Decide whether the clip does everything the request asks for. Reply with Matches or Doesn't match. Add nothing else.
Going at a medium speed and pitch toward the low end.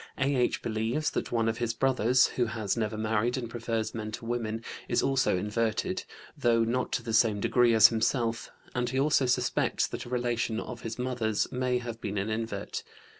Matches